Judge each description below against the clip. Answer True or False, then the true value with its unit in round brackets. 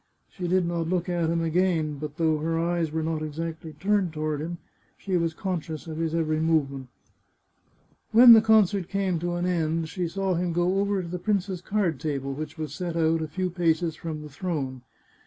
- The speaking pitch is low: False (165 Hz)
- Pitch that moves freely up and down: False (2.4 semitones)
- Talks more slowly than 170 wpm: False (200 wpm)